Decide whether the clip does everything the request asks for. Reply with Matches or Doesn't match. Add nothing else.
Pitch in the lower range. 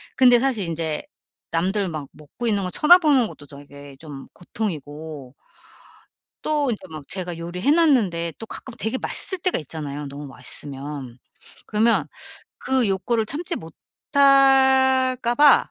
Doesn't match